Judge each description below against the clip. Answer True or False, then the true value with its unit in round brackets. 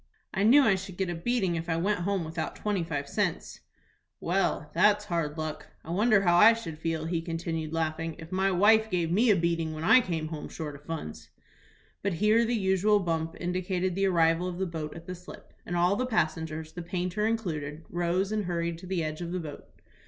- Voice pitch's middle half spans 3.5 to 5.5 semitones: False (3.1 semitones)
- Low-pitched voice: False (175 Hz)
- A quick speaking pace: True (215 wpm)